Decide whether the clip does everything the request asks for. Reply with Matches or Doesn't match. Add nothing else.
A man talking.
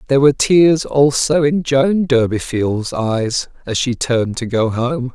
Matches